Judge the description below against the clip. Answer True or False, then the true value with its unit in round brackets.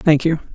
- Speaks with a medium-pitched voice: True (160 Hz)